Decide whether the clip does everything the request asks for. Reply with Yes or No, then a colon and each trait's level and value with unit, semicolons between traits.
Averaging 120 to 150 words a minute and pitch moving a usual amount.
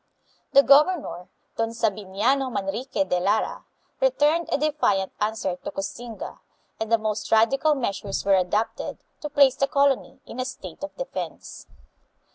No: average, 140 wpm; wide, 5.8 semitones